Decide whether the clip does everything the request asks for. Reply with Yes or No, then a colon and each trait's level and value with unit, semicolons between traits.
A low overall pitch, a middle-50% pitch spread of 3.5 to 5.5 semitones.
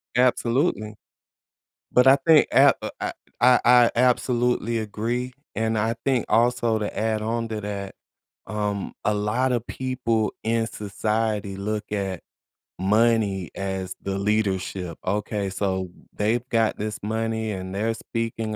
No: low, 110 Hz; narrow, 2.5 semitones